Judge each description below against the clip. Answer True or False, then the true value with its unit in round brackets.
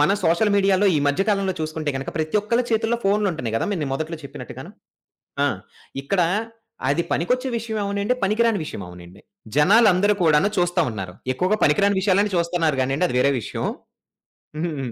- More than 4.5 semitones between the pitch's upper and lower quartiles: True (5.5 semitones)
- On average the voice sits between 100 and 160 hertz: False (180 Hz)